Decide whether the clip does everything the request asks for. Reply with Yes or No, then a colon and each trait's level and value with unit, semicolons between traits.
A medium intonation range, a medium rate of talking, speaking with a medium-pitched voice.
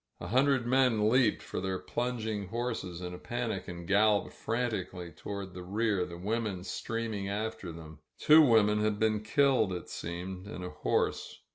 No: average, 4.0 semitones; average, 170 wpm; low, 105 Hz